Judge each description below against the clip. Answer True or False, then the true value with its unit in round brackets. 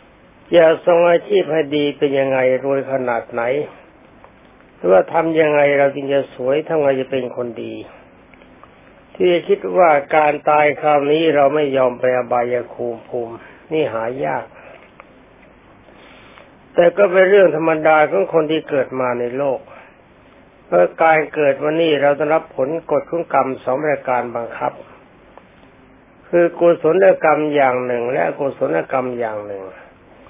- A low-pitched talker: False (145 Hz)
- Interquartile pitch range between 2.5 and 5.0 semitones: True (4.0 semitones)